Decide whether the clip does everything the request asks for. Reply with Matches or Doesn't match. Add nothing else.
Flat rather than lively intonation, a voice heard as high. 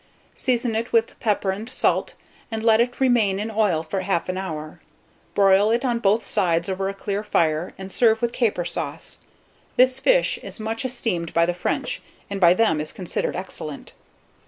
Doesn't match